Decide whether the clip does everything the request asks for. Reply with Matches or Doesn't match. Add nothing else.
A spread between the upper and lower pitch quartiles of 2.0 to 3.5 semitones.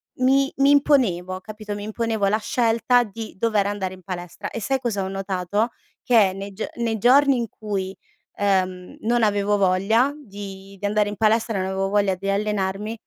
Matches